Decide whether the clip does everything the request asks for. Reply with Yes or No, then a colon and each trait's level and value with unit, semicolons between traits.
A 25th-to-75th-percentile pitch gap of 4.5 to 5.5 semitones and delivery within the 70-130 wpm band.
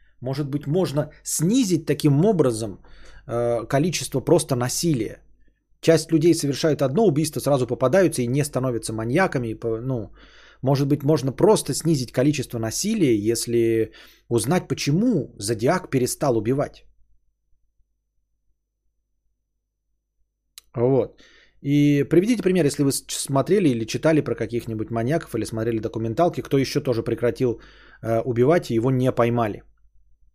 Yes: average, 5.2 semitones; slow, 115 wpm